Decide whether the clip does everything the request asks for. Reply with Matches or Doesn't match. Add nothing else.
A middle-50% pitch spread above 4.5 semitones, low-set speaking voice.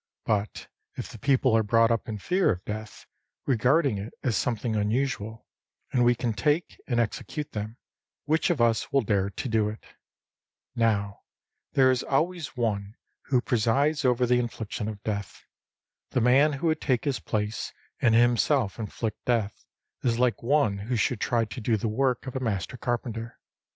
Doesn't match